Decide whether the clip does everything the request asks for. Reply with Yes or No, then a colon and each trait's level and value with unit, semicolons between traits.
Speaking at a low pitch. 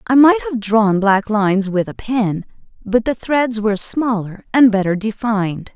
No: high, 220 Hz